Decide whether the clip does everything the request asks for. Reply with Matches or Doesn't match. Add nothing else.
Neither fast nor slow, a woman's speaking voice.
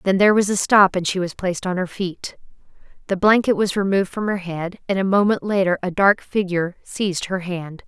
Doesn't match